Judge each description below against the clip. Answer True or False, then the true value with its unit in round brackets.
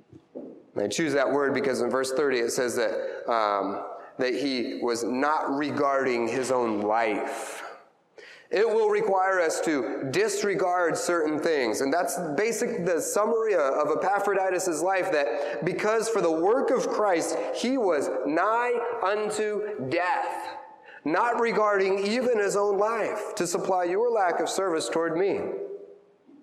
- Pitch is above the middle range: True (205 Hz)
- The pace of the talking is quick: False (140 wpm)